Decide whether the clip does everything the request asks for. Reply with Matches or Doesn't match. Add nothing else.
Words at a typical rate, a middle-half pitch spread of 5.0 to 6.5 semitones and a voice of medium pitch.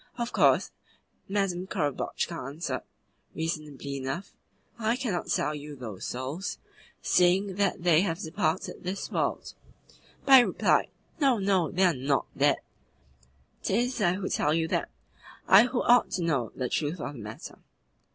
Matches